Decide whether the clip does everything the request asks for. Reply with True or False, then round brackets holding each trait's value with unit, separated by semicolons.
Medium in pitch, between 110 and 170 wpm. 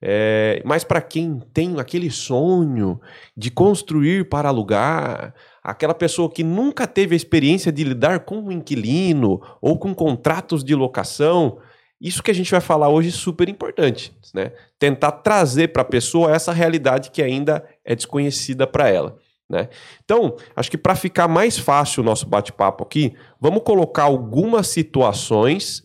True (155 Hz; 160 wpm)